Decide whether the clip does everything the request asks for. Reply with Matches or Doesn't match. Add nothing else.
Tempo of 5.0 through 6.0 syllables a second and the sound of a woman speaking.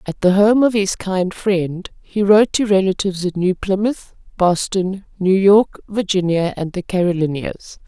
Doesn't match